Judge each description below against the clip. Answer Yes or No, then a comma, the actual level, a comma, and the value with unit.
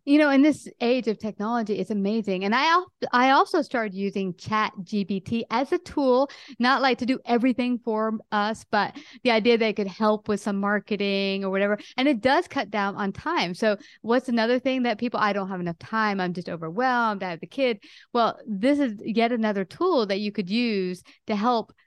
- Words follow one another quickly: Yes, fast, 210 wpm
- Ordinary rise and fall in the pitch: Yes, average, 3.7 semitones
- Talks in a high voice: Yes, high, 220 Hz